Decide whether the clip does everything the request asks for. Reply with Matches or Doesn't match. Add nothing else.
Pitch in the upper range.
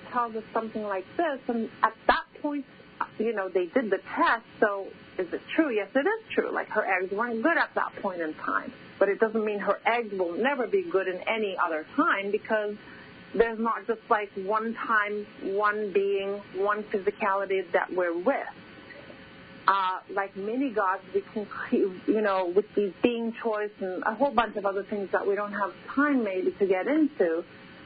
Matches